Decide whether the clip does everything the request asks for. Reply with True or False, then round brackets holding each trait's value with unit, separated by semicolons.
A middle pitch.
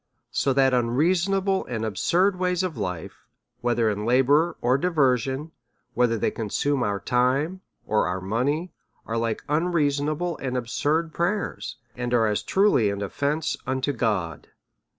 False (130 Hz)